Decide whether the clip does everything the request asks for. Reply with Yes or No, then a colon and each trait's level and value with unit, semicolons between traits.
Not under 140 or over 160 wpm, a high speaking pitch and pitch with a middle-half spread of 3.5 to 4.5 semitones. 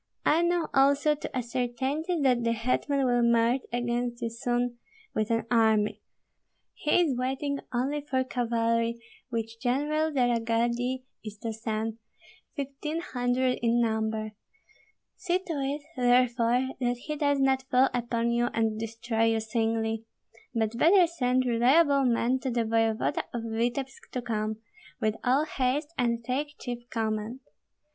No: average, 150 wpm; high, 245 Hz; average, 2.8 semitones